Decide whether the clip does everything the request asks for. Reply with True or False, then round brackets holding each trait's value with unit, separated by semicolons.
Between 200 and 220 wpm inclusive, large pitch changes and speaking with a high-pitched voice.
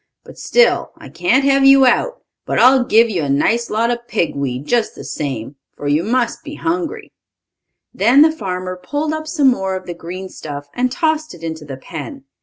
True (205 wpm; 8.4 semitones; 230 Hz)